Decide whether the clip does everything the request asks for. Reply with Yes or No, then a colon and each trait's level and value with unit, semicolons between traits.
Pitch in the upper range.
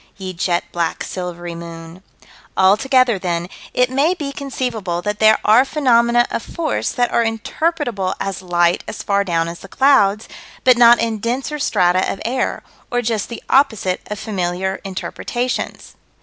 Yes: high, 215 Hz